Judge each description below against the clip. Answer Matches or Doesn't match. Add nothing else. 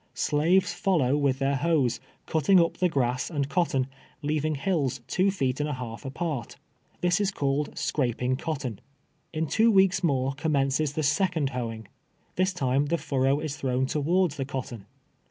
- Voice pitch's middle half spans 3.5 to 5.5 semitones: Matches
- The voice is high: Doesn't match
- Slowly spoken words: Doesn't match